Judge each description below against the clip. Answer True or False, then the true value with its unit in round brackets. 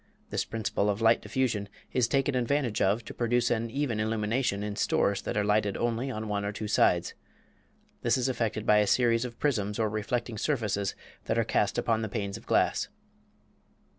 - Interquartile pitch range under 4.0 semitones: True (2.6 semitones)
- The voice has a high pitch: False (110 Hz)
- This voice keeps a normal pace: True (190 wpm)